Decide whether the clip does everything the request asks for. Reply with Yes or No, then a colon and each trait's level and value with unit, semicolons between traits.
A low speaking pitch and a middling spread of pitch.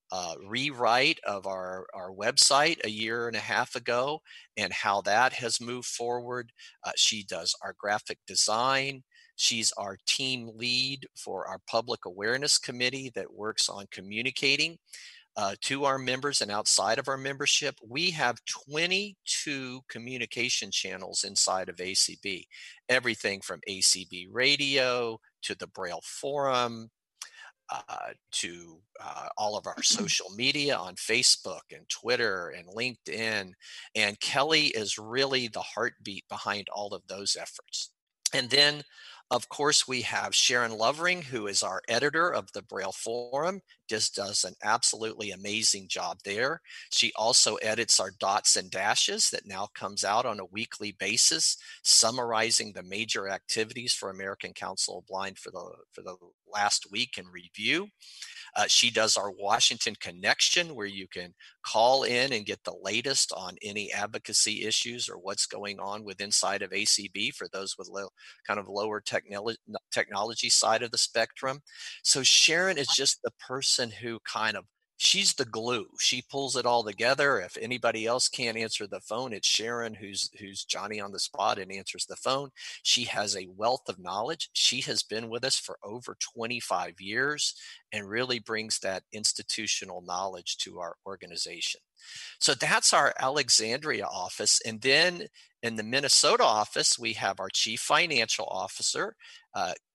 Yes: low, 120 Hz; average, 4.4 semitones